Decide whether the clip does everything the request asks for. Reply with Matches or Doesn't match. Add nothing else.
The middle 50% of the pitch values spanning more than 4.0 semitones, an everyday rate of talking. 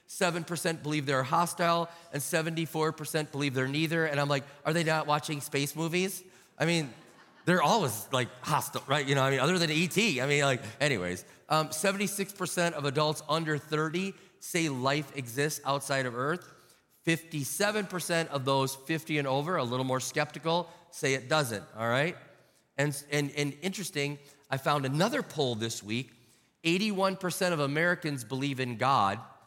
Doesn't match